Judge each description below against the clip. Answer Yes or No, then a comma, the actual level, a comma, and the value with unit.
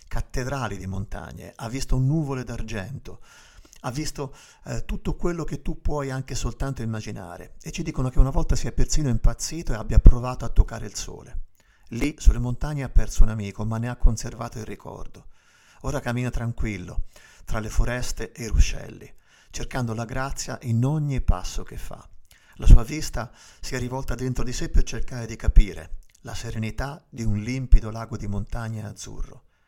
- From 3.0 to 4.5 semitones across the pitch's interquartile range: Yes, average, 3.5 semitones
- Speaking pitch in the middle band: No, low, 120 Hz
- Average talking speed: No, fast, 175 wpm